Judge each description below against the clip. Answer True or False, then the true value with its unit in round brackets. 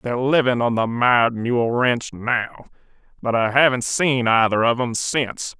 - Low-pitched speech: True (120 Hz)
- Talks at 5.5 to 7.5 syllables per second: False (4.7 syllables/s)